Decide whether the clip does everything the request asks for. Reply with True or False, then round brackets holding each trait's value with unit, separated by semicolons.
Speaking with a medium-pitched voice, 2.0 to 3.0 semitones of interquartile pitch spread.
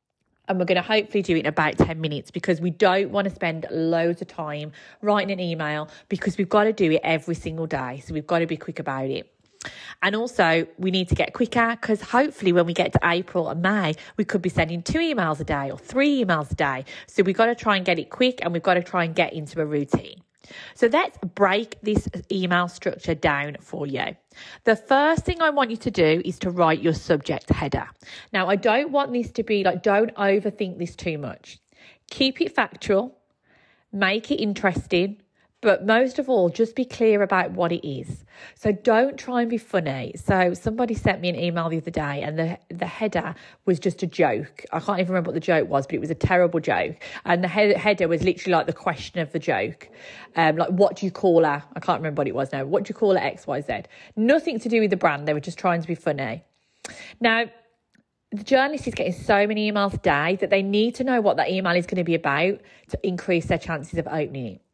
False (180 Hz; 4.3 semitones)